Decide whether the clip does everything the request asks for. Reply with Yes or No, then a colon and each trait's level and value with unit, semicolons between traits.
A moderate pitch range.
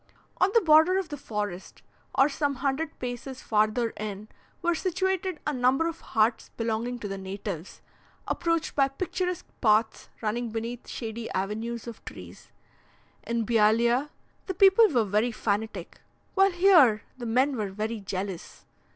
No: wide, 6.2 semitones